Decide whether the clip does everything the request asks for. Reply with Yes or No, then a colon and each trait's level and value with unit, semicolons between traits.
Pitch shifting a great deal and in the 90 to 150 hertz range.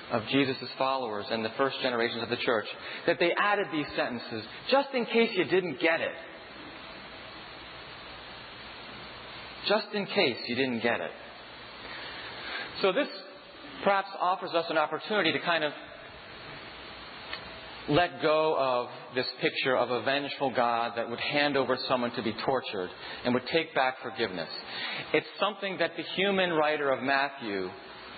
Yes: wide, 5.8 semitones; medium, 140 Hz